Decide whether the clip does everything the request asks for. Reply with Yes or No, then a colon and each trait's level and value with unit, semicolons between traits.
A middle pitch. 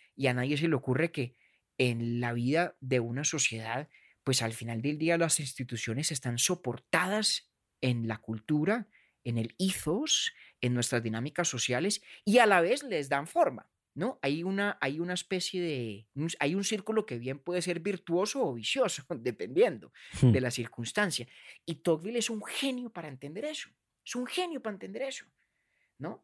Yes: medium, 150 Hz